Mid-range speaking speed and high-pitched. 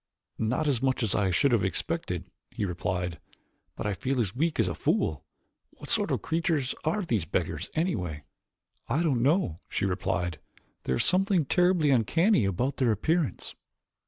No: average, 165 wpm; low, 125 Hz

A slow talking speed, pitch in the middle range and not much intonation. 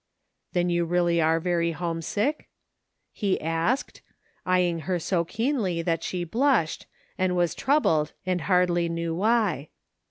No: average, 145 wpm; medium, 175 Hz; narrow, 2.3 semitones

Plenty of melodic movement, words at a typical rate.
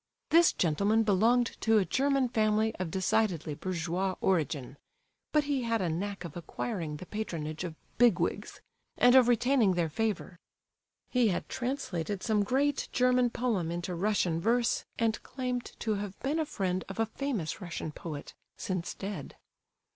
Yes: wide, 5.7 semitones; average, 155 wpm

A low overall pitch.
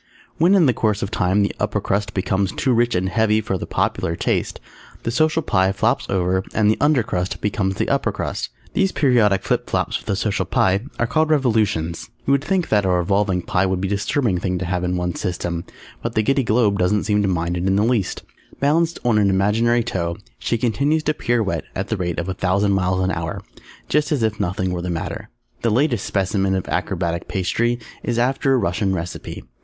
Yes: low, 100 Hz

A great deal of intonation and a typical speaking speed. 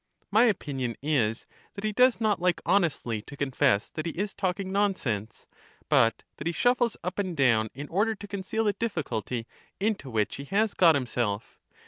Yes: wide, 8.5 semitones; average, 185 wpm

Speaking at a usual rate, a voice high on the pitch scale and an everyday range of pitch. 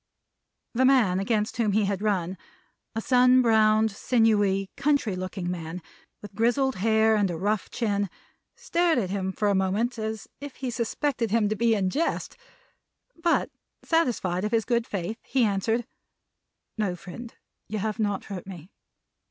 Yes: average, 160 wpm; high, 215 Hz; average, 3.5 semitones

